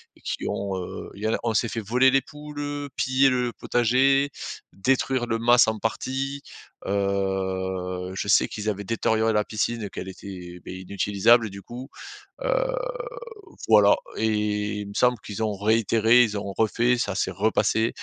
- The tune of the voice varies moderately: Yes, average, 3.7 semitones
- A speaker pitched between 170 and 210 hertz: No, low, 110 Hz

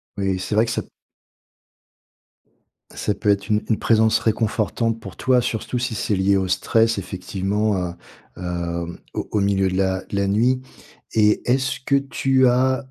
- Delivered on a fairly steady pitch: No, average, 3.4 semitones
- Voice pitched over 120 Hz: No, low, 105 Hz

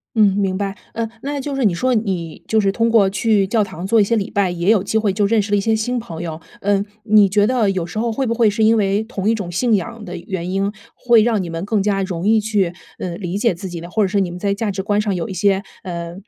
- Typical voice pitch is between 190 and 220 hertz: Yes, high, 205 Hz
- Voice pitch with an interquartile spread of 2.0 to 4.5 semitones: Yes, average, 2.8 semitones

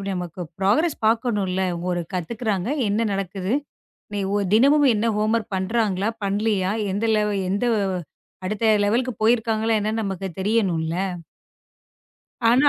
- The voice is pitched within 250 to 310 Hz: No, high, 210 Hz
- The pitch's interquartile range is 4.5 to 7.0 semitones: No, average, 3.0 semitones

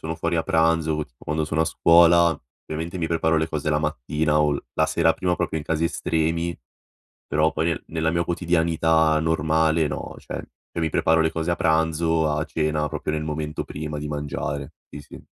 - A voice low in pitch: Yes, very low, 80 Hz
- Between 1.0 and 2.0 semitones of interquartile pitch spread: Yes, narrow, 1.3 semitones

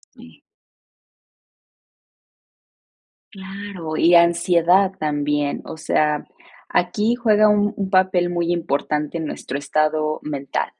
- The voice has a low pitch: No, medium, 170 Hz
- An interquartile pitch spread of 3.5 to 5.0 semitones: Yes, average, 3.8 semitones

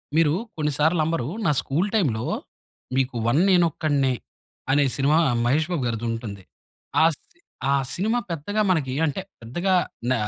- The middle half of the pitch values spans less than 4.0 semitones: No, average, 4.6 semitones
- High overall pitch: No, medium, 150 Hz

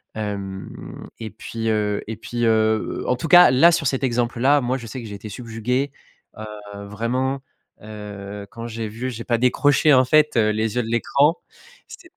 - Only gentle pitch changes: No, average, 3.1 semitones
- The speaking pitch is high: No, low, 115 Hz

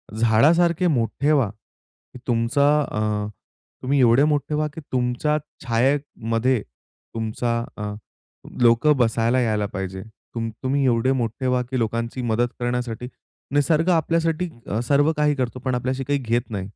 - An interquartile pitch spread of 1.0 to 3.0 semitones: No, average, 3.9 semitones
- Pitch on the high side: No, low, 125 Hz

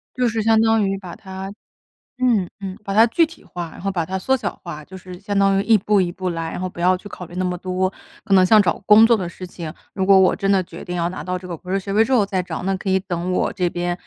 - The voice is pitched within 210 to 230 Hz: No, high, 190 Hz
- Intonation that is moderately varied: No, narrow, 2.1 semitones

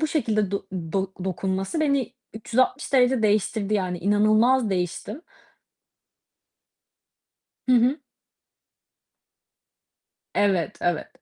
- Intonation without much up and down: No, average, 4.9 semitones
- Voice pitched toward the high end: Yes, high, 215 Hz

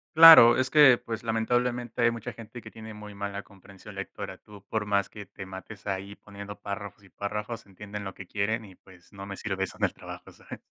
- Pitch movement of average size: No, narrow, 2.3 semitones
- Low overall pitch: Yes, low, 105 Hz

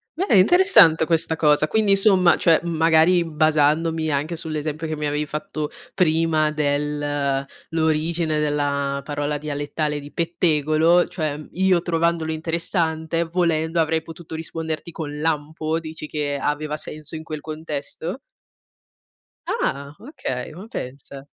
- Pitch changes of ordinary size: No, narrow, 1.9 semitones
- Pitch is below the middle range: No, medium, 155 Hz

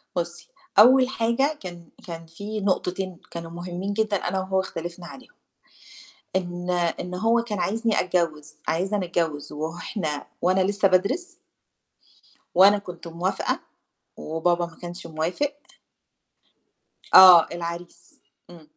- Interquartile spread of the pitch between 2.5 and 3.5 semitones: Yes, average, 3.0 semitones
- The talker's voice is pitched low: No, medium, 180 Hz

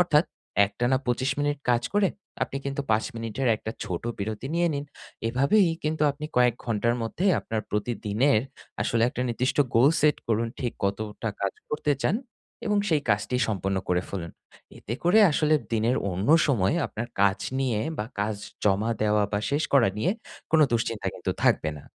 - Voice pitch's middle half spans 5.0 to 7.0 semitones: Yes, average, 5.3 semitones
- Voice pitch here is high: No, low, 115 Hz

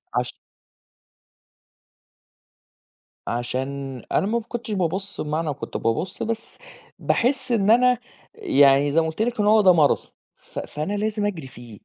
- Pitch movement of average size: No, wide, 7.7 semitones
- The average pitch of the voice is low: No, high, 190 Hz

